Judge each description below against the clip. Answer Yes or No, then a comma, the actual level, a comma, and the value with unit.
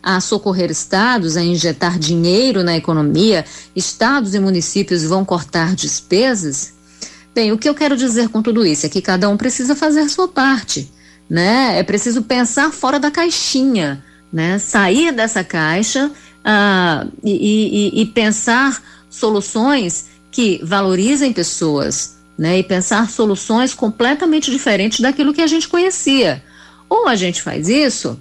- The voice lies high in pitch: Yes, high, 210 Hz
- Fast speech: No, average, 145 wpm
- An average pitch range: No, wide, 6.7 semitones